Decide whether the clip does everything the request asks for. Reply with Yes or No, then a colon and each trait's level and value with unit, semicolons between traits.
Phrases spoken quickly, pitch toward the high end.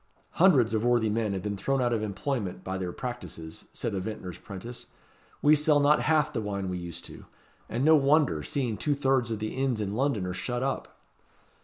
No: fast, 210 wpm; low, 115 Hz